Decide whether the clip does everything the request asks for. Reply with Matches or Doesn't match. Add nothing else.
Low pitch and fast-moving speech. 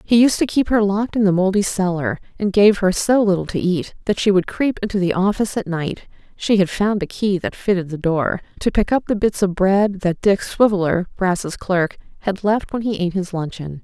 Doesn't match